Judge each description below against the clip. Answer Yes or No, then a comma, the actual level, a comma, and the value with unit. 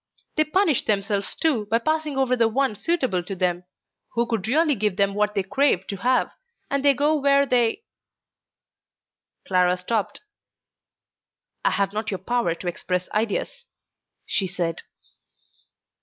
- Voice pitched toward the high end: Yes, high, 220 Hz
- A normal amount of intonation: No, wide, 6.2 semitones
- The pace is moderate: Yes, average, 150 wpm